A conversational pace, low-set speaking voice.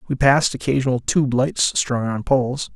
Yes: average, 175 wpm; low, 130 Hz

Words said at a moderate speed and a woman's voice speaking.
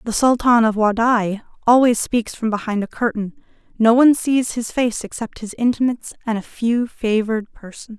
Yes: average, 175 wpm; female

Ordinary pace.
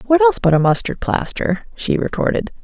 Yes: average, 180 wpm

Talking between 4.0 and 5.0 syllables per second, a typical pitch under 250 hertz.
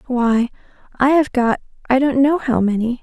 No: 4.7 syllables/s; very high, 255 Hz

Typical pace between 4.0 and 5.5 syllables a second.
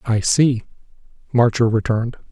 Yes: 5.0 syllables/s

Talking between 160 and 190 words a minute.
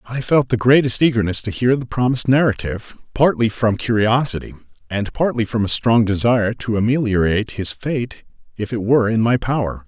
Yes: average, 175 wpm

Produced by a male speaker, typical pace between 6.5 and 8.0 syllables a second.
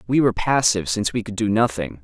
Yes: male; 7.0 syllables/s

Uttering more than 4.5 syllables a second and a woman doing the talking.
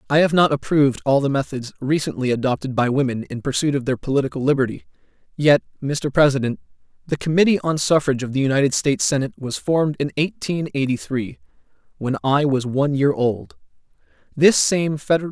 No: 6.1 syllables/s; male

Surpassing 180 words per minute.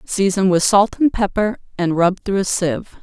Yes: average, 200 wpm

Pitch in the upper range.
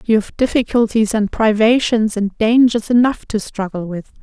Yes: high, 220 Hz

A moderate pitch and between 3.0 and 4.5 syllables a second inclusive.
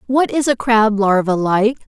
No: high, 225 Hz; 4.4 syllables/s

